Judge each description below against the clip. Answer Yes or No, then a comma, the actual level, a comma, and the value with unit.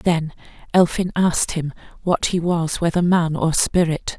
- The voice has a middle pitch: Yes, medium, 170 Hz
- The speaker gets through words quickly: No, average, 160 wpm